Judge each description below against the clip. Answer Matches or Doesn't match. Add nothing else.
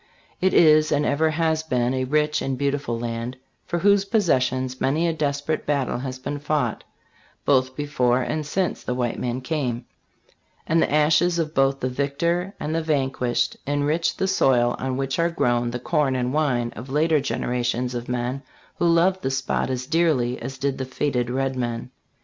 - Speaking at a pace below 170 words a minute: Doesn't match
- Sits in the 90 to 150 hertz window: Matches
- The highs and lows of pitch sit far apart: Doesn't match